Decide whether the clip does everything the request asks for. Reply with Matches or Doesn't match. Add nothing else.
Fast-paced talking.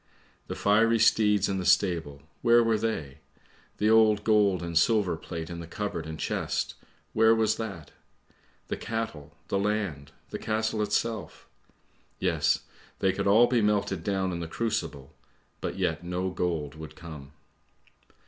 Doesn't match